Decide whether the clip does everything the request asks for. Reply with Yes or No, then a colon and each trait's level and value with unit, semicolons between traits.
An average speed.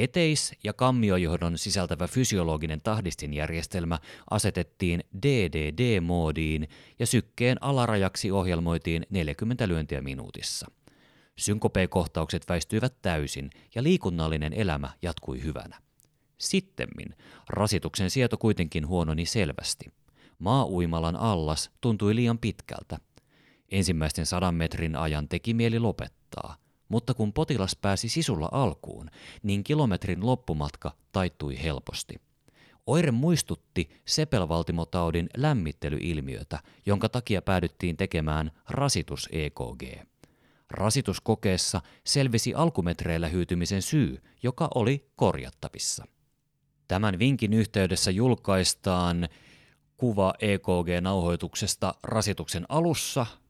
No: slow, 85 wpm